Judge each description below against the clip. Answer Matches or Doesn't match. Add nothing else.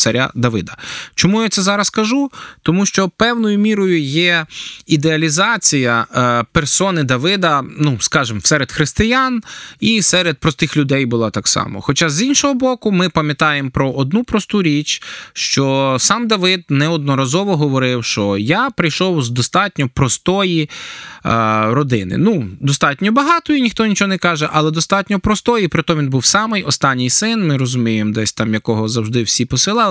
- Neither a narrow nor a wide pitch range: Doesn't match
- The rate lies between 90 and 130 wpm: Doesn't match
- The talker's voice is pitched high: Doesn't match